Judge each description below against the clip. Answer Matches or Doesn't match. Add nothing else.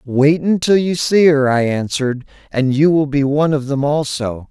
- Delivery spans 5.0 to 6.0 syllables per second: Doesn't match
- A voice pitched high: Doesn't match